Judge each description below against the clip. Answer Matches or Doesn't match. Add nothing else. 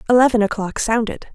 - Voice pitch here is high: Matches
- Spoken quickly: Doesn't match